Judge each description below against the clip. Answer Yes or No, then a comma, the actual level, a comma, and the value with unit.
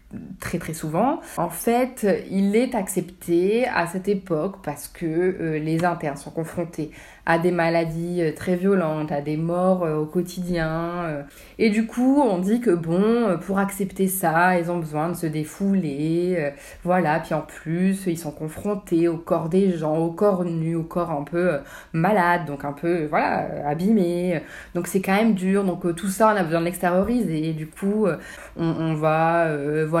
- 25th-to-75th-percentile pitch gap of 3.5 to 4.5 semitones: No, average, 3.1 semitones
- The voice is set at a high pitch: No, medium, 175 Hz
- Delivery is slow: No, average, 190 wpm